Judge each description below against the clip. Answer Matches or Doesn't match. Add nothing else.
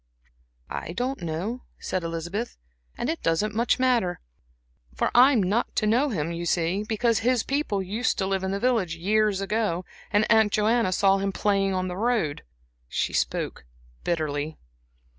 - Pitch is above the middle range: Matches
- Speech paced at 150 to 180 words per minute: Matches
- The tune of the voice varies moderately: Matches